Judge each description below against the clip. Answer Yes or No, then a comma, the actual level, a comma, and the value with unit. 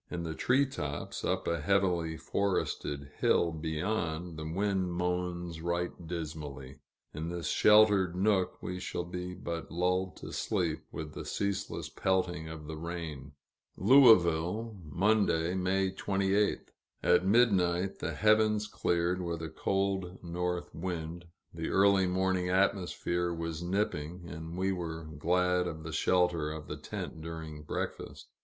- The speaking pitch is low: Yes, very low, 90 Hz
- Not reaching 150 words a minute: Yes, slow, 135 wpm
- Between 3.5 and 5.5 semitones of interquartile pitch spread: No, average, 2.7 semitones